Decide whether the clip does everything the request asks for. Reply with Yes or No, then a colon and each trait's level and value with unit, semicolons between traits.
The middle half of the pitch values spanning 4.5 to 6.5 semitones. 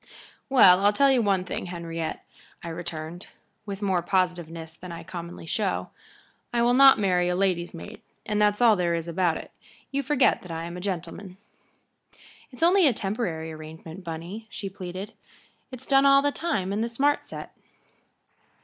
Yes: average, 5.1 semitones